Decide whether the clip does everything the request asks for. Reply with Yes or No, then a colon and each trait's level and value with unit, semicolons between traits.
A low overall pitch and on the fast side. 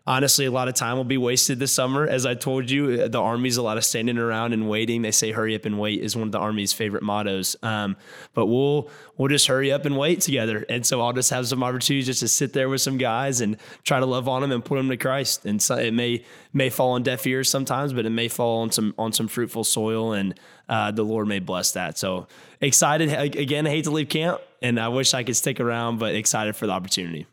Yes: low, 125 Hz; fast, 260 wpm